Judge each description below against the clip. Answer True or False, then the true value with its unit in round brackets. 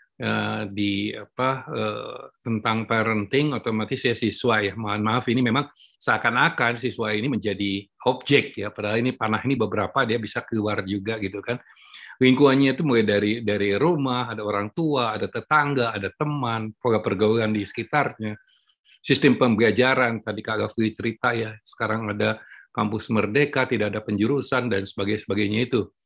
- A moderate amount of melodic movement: True (3.1 semitones)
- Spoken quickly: True (145 wpm)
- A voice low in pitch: True (110 Hz)